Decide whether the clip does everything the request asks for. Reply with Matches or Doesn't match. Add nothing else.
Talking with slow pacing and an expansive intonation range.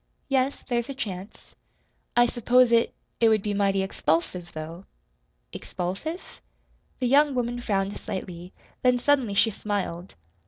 Doesn't match